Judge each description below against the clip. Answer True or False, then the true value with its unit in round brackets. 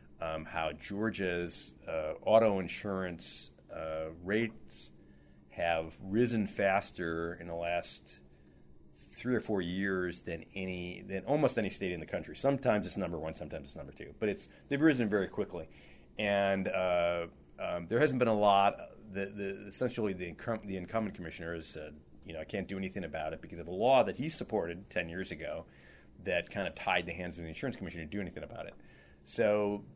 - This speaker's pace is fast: False (185 wpm)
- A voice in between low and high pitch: False (90 Hz)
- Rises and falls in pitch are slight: False (3.8 semitones)